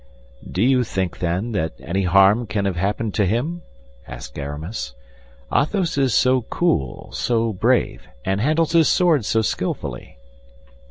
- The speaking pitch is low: Yes, low, 110 Hz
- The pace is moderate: Yes, average, 145 wpm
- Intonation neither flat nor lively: No, wide, 5.7 semitones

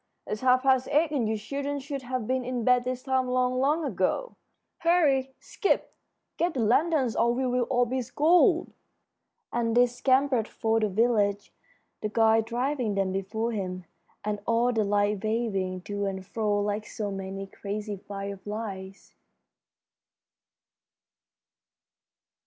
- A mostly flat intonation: No, average, 4.0 semitones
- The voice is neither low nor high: No, high, 230 Hz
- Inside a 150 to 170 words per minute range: No, average, 140 wpm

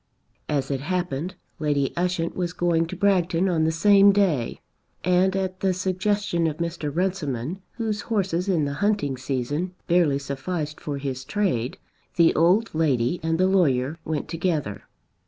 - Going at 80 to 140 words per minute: No, average, 155 wpm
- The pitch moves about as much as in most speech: Yes, average, 4.4 semitones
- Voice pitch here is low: No, medium, 170 Hz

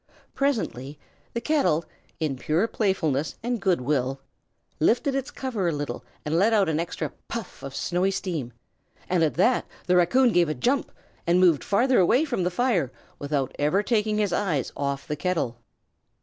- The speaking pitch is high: No, medium, 180 Hz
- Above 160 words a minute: Yes, average, 170 wpm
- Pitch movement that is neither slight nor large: No, wide, 7.0 semitones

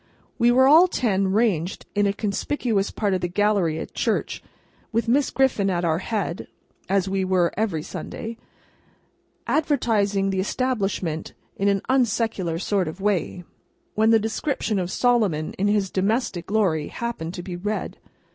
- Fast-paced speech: No, average, 145 wpm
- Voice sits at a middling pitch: No, high, 200 Hz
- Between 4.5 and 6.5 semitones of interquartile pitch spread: No, average, 3.7 semitones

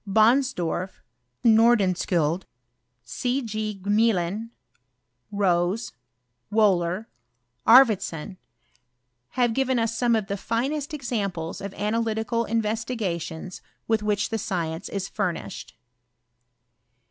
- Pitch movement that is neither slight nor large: Yes, average, 3.7 semitones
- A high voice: Yes, high, 210 Hz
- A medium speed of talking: No, slow, 90 wpm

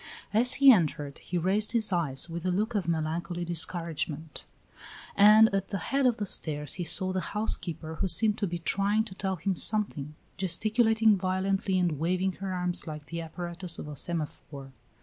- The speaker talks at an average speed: Yes, average, 180 wpm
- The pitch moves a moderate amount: Yes, average, 3.9 semitones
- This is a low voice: No, medium, 180 Hz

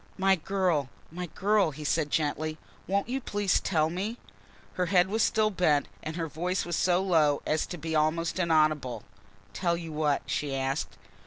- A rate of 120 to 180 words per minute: Yes, average, 175 wpm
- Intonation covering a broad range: No, average, 3.5 semitones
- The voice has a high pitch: No, medium, 165 Hz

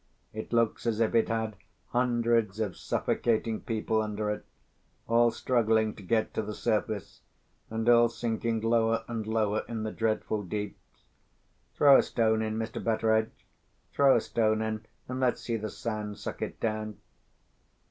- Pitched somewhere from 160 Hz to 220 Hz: No, low, 110 Hz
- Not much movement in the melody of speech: Yes, narrow, 1.3 semitones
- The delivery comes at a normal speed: Yes, average, 155 wpm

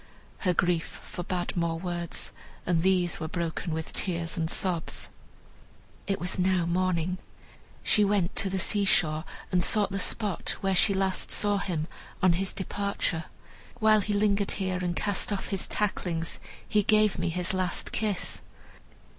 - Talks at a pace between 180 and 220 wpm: No, average, 155 wpm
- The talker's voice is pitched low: No, medium, 185 Hz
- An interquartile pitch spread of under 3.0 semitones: Yes, narrow, 2.6 semitones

